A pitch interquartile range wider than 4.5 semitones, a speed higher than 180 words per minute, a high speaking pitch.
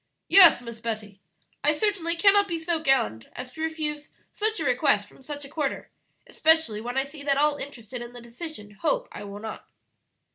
Yes: wide, 5.6 semitones; average, 190 wpm; very high, 285 Hz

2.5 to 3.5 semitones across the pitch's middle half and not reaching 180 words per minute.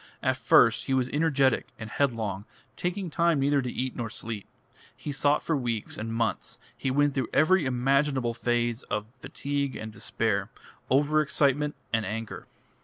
No: average, 4.0 semitones; average, 160 wpm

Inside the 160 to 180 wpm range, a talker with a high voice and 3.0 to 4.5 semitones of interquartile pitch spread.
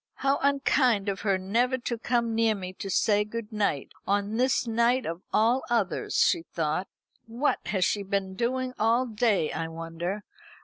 Yes: average, 170 wpm; high, 215 Hz; average, 4.0 semitones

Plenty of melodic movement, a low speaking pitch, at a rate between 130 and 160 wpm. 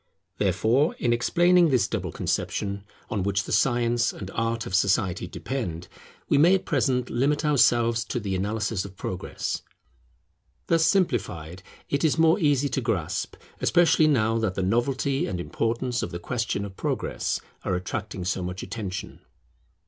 Yes: wide, 6.0 semitones; low, 115 Hz; average, 155 wpm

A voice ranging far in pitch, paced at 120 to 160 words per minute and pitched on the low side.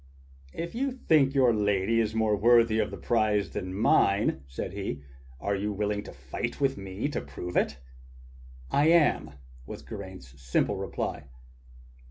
No: average, 4.2 semitones; average, 150 wpm; low, 105 Hz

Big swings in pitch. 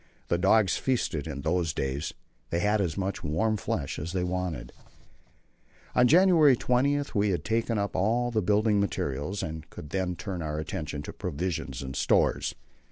Yes: wide, 5.7 semitones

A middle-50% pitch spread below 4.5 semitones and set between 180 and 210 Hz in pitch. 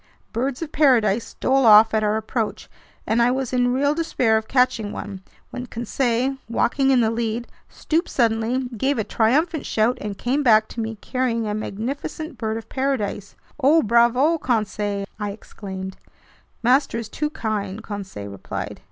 No: average, 3.6 semitones; high, 230 Hz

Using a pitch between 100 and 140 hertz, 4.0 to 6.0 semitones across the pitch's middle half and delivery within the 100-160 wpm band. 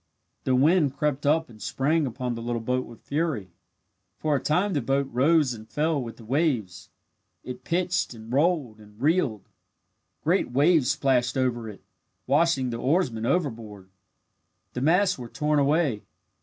Yes: low, 135 Hz; average, 4.9 semitones; average, 155 wpm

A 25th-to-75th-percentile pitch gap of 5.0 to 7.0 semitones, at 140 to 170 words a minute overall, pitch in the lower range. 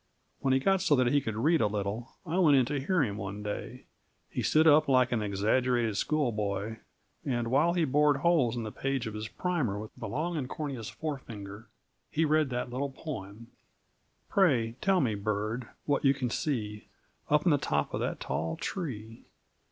No: wide, 5.6 semitones; average, 190 wpm; low, 125 Hz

